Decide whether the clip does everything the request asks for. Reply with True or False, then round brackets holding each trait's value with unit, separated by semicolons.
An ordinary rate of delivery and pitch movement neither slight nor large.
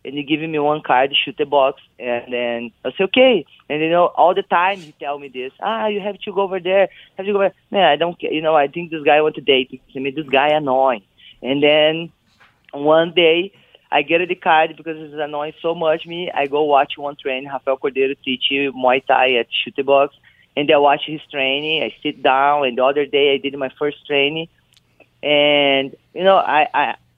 False (235 wpm; 3.1 semitones)